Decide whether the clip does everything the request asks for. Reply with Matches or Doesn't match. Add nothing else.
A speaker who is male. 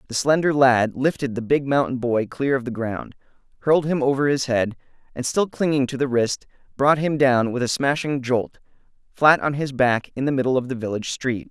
Matches